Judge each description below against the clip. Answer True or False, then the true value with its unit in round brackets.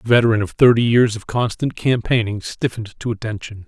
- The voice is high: False (110 Hz)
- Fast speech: False (180 wpm)